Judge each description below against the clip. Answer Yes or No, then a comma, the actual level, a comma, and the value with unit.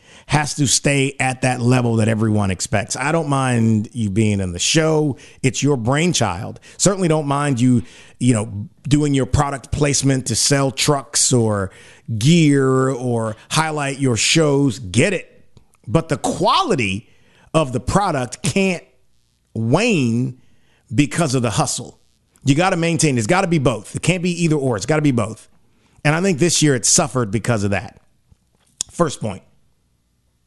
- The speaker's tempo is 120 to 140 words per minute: No, average, 165 wpm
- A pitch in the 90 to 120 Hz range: No, low, 130 Hz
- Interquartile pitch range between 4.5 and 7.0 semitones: Yes, average, 5.0 semitones